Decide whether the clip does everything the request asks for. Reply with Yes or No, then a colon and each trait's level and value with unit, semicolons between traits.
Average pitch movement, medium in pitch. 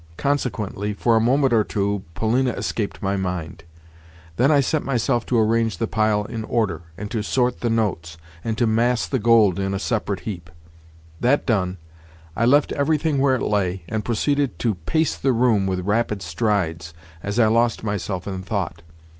No: average, 3.8 semitones; low, 110 Hz